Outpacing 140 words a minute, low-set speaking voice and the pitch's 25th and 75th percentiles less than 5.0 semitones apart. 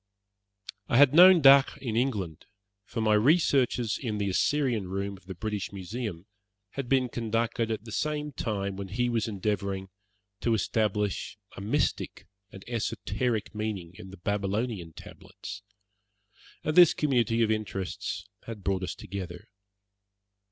No: slow, 135 wpm; low, 110 Hz; average, 3.8 semitones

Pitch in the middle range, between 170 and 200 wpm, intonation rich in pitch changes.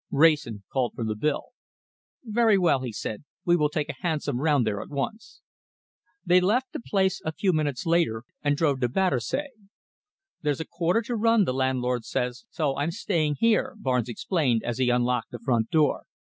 Yes: medium, 150 Hz; average, 185 wpm; wide, 6.4 semitones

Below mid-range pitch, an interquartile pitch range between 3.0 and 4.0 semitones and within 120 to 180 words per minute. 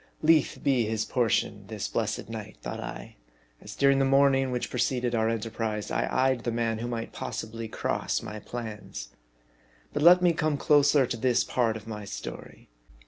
Yes: low, 120 Hz; average, 3.4 semitones; average, 175 wpm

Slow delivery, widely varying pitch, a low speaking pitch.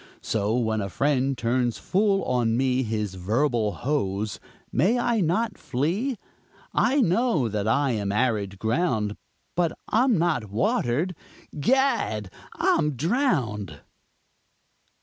Yes: slow, 115 wpm; wide, 8.4 semitones; low, 130 Hz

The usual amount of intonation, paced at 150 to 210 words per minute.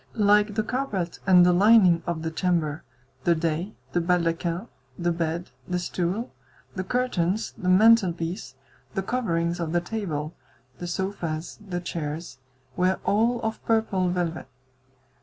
No: average, 3.3 semitones; average, 140 wpm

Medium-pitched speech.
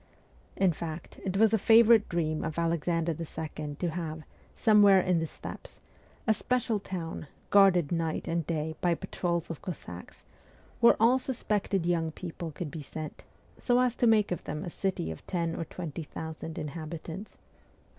Yes: medium, 170 Hz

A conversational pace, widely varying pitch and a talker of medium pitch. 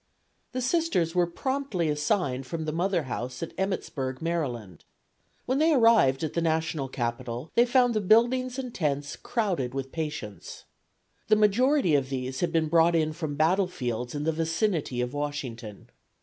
Yes: average, 160 wpm; wide, 7.6 semitones; medium, 160 Hz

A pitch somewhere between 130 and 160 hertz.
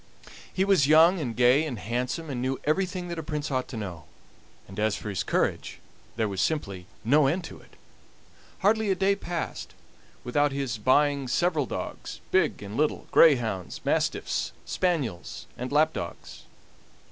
Yes: medium, 140 Hz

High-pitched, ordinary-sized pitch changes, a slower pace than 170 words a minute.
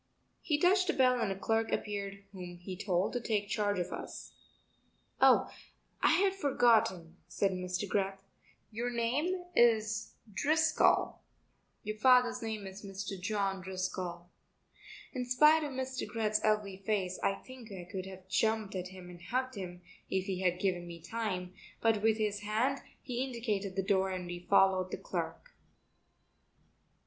Yes: high, 205 Hz; average, 4.1 semitones; average, 155 wpm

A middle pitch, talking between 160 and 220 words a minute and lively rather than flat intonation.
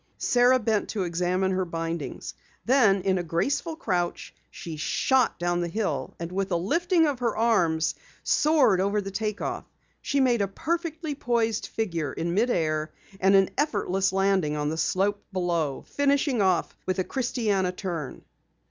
No: high, 195 Hz; average, 165 wpm; wide, 5.7 semitones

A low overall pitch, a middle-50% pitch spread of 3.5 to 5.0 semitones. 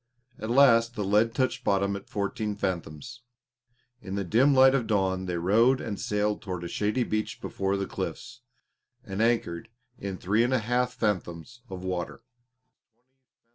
Yes: low, 105 Hz; average, 3.9 semitones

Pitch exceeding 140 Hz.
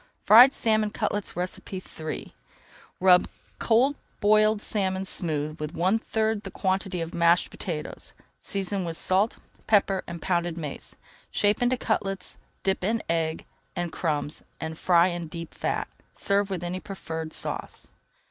Yes: medium, 185 Hz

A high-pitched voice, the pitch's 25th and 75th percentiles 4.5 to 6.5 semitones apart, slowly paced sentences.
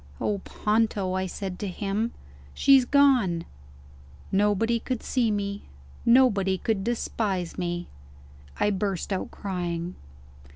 No: high, 200 Hz; average, 3.3 semitones; slow, 115 wpm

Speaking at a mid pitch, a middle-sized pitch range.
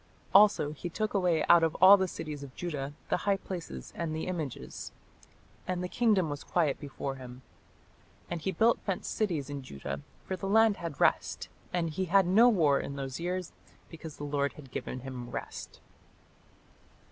Yes: medium, 165 Hz; average, 5.0 semitones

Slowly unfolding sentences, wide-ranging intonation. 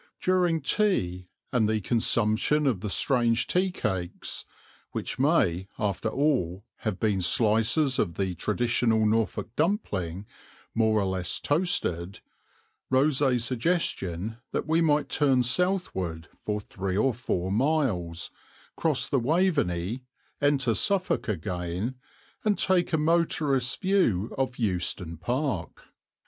Yes: slow, 120 wpm; wide, 7.8 semitones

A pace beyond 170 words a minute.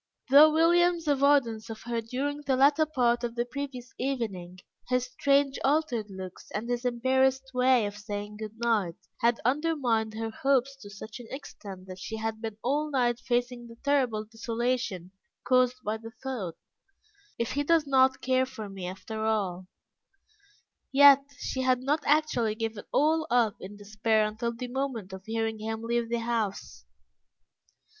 No: average, 160 wpm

